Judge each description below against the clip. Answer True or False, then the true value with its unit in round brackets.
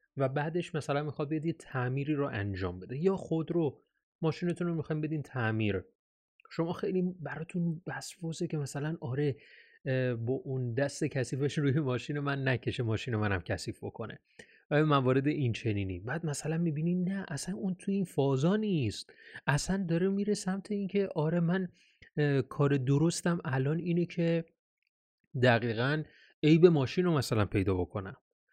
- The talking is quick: False (145 wpm)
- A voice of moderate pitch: True (150 Hz)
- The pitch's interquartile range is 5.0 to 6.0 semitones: False (4.6 semitones)